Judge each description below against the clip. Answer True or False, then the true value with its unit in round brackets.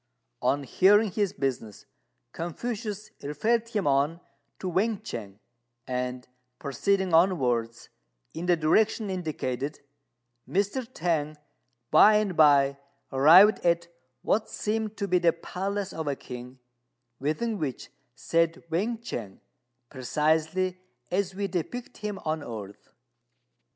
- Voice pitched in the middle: True (170 Hz)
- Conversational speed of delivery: False (115 wpm)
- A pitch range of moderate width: False (6.3 semitones)